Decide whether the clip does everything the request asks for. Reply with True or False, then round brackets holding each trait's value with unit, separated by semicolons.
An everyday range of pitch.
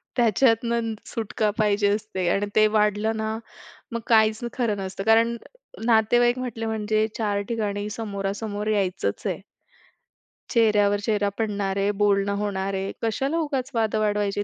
False (1.8 semitones)